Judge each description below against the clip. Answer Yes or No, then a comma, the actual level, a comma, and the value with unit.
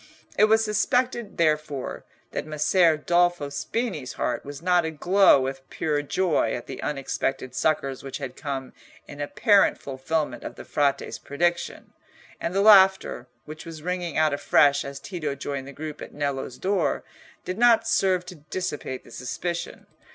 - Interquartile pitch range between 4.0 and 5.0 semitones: Yes, average, 4.6 semitones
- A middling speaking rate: Yes, average, 155 wpm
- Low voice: No, medium, 155 Hz